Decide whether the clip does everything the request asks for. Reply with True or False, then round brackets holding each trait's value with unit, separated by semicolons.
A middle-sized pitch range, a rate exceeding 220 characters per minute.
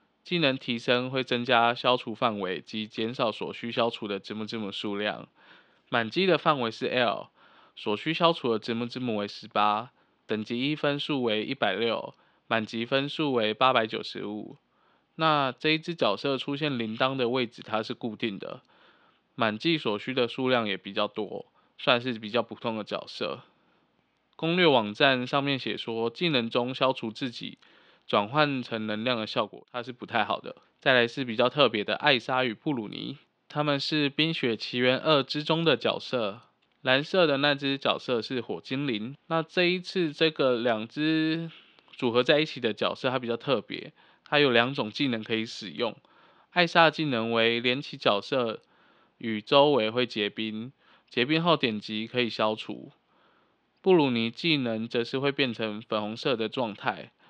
True (4.5 semitones; 250 characters per minute)